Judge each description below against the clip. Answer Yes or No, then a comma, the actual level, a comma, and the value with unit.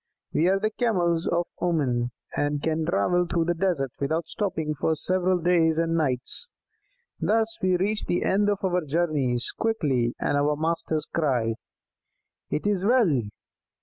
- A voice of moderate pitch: Yes, medium, 165 Hz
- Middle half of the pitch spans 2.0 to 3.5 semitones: No, average, 4.0 semitones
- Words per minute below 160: Yes, average, 150 wpm